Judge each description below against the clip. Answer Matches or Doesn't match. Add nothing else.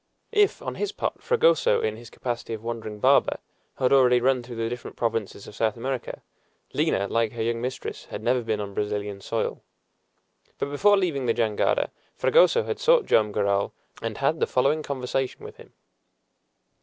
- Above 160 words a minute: Matches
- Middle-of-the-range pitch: Doesn't match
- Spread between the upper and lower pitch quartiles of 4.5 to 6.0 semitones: Doesn't match